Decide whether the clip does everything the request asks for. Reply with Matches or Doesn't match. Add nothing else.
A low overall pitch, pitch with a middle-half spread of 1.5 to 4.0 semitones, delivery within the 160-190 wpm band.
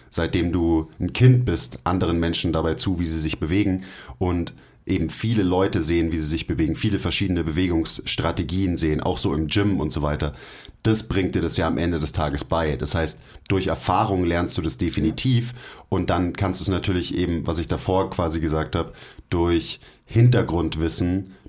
Matches